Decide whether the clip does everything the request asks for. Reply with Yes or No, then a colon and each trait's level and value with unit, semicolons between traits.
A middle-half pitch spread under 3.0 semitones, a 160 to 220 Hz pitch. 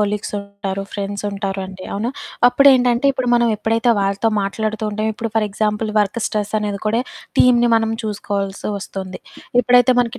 Yes: narrow, 2.6 semitones; high, 210 Hz